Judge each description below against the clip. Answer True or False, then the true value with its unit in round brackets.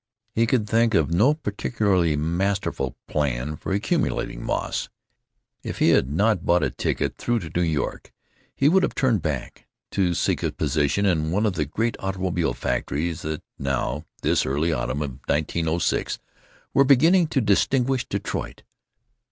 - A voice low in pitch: True (90 Hz)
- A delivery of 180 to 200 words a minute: False (155 wpm)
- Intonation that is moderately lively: False (6.9 semitones)